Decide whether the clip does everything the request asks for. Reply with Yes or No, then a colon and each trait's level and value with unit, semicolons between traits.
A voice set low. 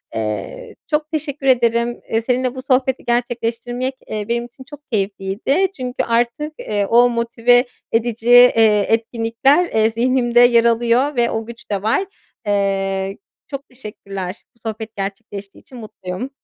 No: high, 235 Hz